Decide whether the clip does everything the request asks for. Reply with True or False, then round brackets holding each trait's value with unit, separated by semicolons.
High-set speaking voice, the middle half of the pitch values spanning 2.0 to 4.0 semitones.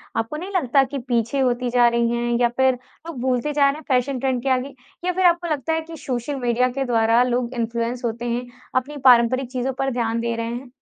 True (250 Hz; 2.4 semitones)